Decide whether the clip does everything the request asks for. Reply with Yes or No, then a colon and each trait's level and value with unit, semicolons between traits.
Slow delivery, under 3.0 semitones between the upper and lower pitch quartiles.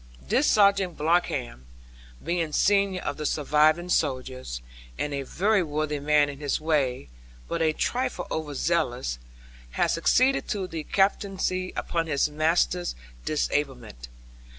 No: slow, 130 wpm; average, 4.1 semitones